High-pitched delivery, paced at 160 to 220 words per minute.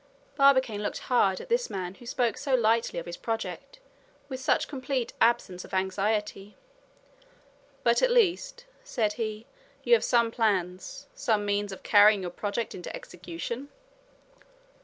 No: high, 225 Hz; average, 145 wpm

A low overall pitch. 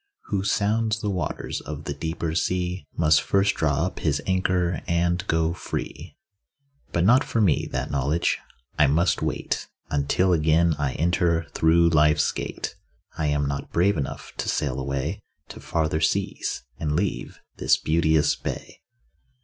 Yes: very low, 80 Hz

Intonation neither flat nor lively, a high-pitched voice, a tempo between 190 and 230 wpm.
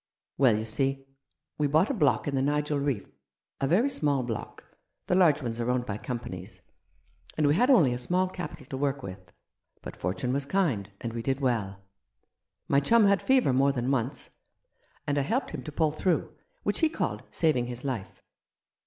No: average, 4.3 semitones; medium, 140 Hz; average, 200 wpm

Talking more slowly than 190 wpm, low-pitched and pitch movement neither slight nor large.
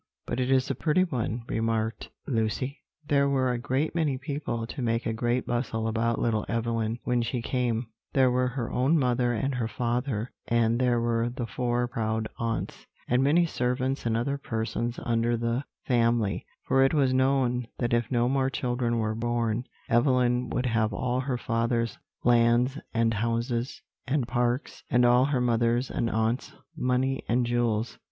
No: average, 170 wpm; low, 120 Hz; narrow, 1.8 semitones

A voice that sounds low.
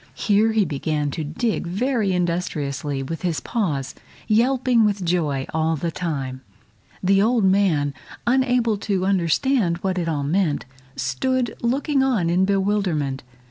No: medium, 185 Hz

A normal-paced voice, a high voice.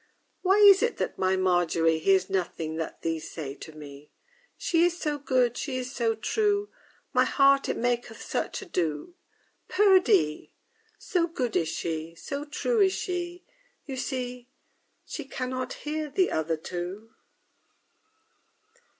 Yes: average, 150 wpm; very high, 250 Hz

